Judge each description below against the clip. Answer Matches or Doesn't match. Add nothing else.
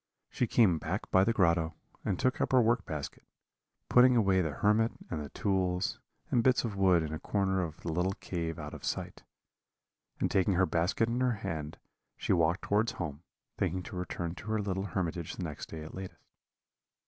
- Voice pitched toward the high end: Doesn't match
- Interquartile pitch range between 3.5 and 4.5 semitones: Matches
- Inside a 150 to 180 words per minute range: Doesn't match